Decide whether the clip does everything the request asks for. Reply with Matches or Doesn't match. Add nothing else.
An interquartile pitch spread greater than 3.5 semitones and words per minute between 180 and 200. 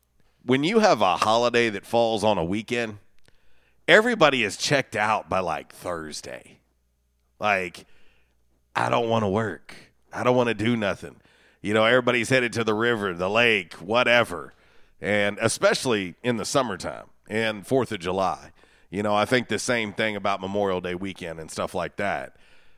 Doesn't match